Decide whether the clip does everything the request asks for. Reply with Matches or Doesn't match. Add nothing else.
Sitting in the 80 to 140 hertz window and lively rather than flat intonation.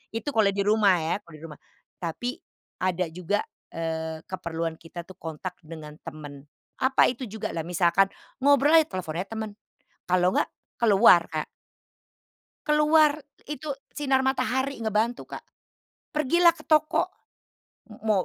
Doesn't match